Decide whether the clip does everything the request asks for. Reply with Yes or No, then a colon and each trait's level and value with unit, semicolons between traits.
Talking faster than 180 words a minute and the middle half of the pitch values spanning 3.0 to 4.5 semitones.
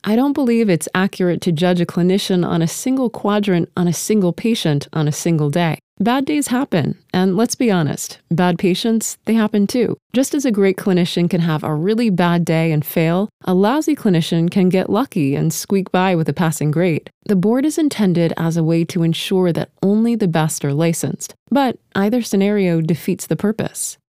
Yes: average, 200 wpm; average, 4.2 semitones